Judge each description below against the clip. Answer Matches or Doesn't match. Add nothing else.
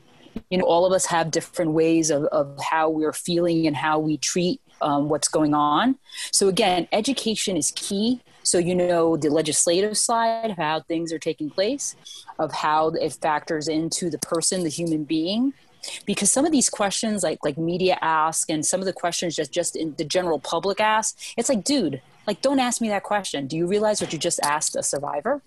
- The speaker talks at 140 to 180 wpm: Doesn't match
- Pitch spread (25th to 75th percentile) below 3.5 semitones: Doesn't match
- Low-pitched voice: Doesn't match